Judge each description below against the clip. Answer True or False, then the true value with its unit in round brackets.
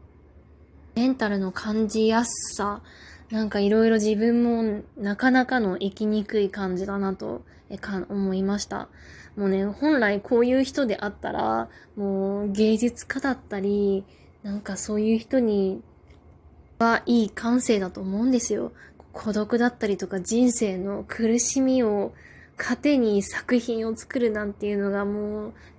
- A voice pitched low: False (210 Hz)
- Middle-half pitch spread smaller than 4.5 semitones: True (2.8 semitones)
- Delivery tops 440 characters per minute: False (270 characters per minute)